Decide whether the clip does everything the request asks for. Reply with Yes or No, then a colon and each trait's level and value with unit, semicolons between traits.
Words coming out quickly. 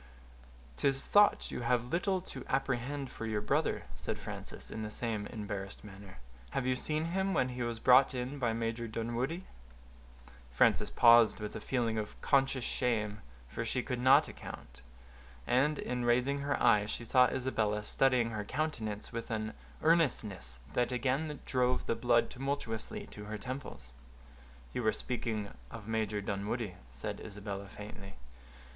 No: average, 155 wpm